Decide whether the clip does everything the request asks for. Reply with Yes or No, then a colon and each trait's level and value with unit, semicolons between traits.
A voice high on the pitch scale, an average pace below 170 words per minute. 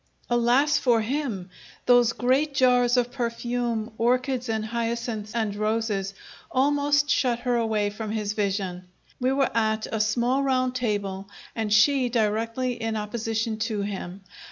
Yes: high, 230 Hz; average, 140 wpm